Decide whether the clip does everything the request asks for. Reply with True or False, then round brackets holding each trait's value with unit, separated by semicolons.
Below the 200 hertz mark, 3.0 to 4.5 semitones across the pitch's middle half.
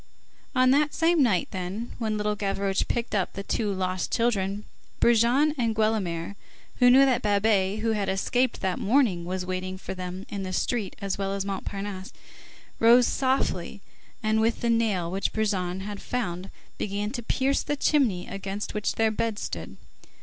False (210 Hz; 3.5 semitones)